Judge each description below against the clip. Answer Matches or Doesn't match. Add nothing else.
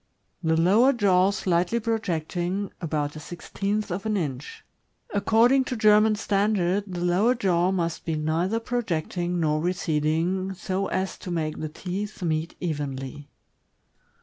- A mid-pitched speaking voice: Matches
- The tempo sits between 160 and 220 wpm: Doesn't match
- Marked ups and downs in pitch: Doesn't match